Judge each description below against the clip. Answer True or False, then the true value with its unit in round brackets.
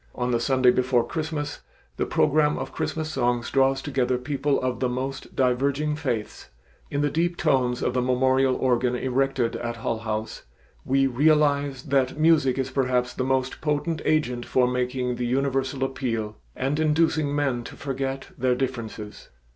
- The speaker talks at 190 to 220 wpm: False (160 wpm)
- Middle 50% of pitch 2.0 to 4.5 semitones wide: True (2.4 semitones)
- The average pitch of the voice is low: True (130 Hz)